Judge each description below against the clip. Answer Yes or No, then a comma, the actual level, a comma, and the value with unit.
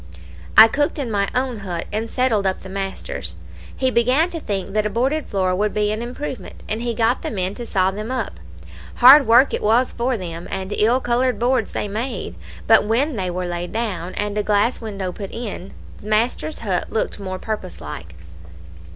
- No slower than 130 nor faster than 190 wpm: No, average, 200 wpm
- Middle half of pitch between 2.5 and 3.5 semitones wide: No, average, 4.2 semitones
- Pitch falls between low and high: No, high, 215 Hz